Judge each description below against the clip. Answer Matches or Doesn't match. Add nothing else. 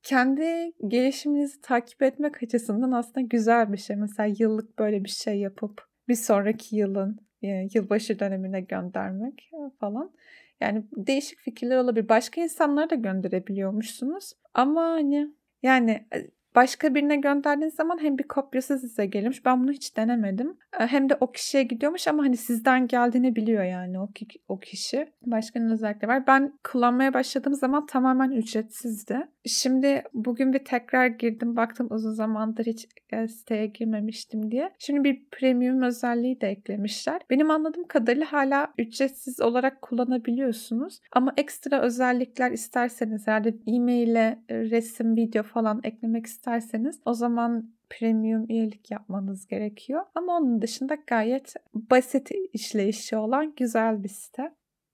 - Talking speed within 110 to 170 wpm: Matches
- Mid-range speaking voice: Doesn't match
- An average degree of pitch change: Matches